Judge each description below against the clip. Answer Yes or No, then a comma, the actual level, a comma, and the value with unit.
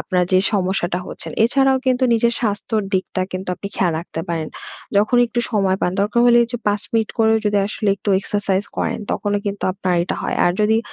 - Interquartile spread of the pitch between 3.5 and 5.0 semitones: No, average, 3.1 semitones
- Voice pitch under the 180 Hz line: No, high, 205 Hz